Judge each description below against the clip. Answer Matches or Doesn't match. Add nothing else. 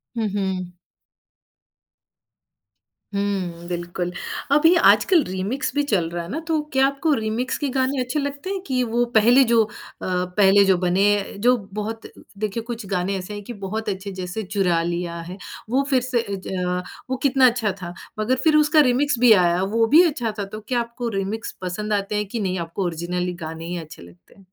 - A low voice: Doesn't match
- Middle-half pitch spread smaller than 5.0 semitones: Doesn't match